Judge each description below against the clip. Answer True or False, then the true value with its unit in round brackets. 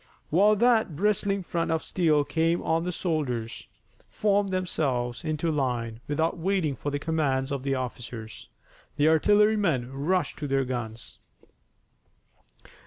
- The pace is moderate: False (130 wpm)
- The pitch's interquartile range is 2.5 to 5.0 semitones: False (5.4 semitones)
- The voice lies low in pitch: False (155 Hz)